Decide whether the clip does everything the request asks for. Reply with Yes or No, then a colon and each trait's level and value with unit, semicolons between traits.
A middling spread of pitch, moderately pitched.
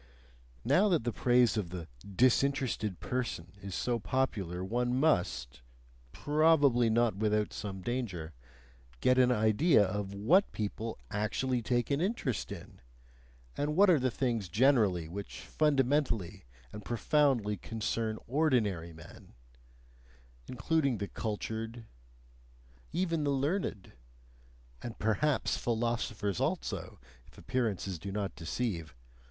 No: average, 4.7 semitones; low, 115 Hz